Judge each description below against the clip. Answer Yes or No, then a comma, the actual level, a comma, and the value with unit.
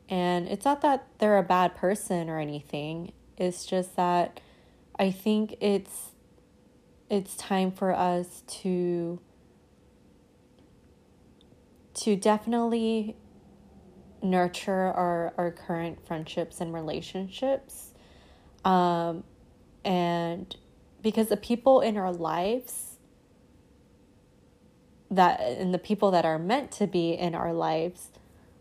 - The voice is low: No, medium, 180 Hz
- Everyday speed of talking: No, slow, 105 wpm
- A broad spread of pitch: No, average, 3.4 semitones